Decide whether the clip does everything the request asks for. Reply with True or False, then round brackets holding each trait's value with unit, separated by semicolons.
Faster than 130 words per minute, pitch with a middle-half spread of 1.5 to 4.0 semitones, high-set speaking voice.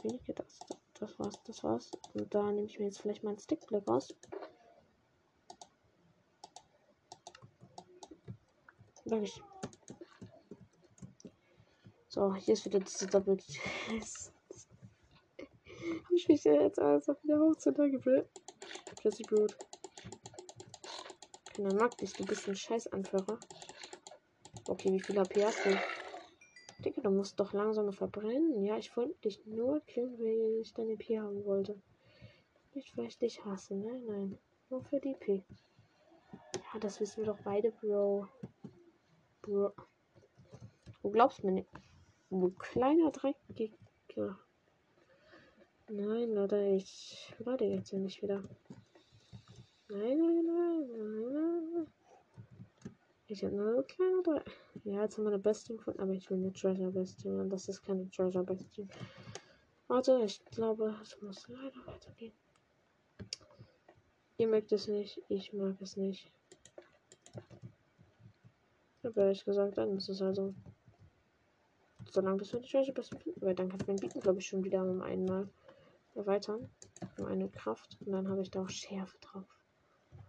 True (140 wpm; 3.5 semitones; 205 Hz)